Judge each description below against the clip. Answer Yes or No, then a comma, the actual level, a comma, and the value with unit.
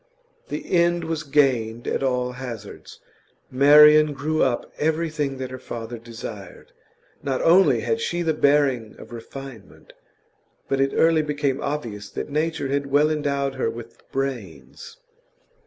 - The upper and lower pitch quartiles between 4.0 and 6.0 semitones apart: No, average, 3.4 semitones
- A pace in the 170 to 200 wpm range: No, average, 140 wpm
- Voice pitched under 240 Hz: Yes, medium, 140 Hz